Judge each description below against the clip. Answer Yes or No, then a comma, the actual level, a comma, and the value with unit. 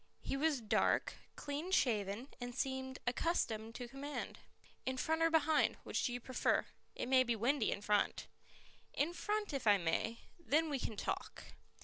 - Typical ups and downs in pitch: Yes, average, 4.6 semitones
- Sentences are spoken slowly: No, average, 165 wpm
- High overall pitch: Yes, very high, 260 Hz